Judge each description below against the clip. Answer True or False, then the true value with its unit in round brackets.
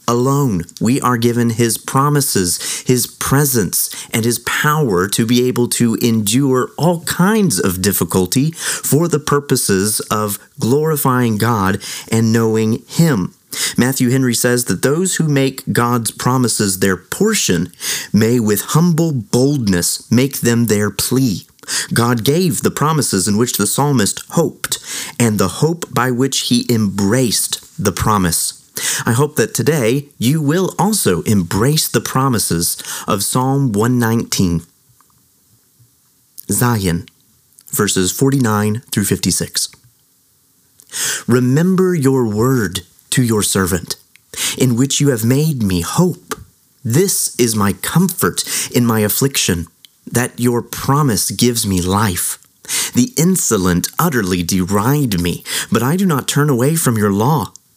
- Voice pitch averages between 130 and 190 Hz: False (120 Hz)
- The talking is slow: True (130 wpm)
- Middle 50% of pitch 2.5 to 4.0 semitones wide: False (4.9 semitones)